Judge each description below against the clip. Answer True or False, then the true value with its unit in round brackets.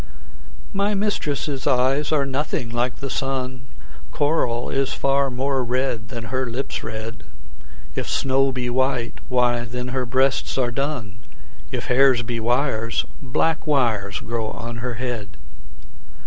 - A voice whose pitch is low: True (125 Hz)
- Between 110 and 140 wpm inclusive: True (135 wpm)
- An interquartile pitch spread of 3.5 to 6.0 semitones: False (2.4 semitones)